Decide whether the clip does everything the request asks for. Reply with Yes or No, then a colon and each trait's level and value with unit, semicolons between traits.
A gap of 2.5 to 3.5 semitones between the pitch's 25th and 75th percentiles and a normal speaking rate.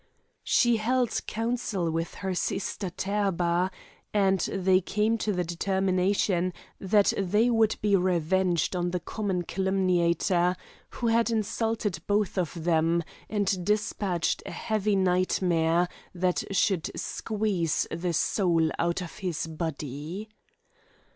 No: average, 3.2 semitones; slow, 120 wpm